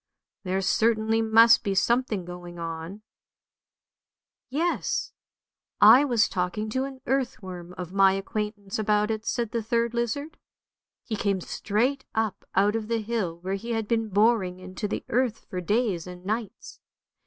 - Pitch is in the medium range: No, high, 215 Hz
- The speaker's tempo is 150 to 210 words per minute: Yes, average, 155 wpm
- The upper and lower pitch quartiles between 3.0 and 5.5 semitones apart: Yes, average, 3.6 semitones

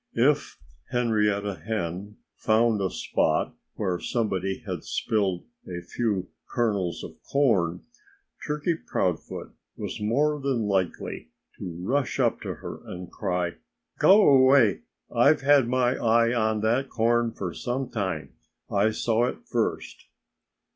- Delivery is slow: Yes, slow, 125 wpm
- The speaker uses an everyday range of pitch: Yes, average, 4.4 semitones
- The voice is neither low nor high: No, low, 110 Hz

